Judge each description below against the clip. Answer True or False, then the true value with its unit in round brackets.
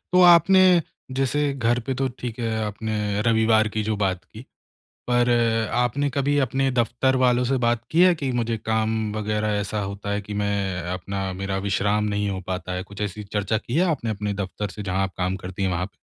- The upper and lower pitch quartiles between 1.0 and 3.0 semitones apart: False (3.7 semitones)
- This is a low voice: True (110 Hz)